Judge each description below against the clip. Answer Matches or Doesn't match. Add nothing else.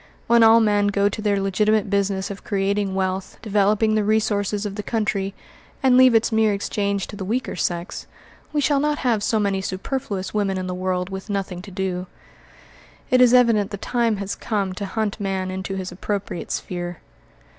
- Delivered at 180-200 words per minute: Matches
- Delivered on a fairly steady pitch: Matches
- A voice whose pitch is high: Matches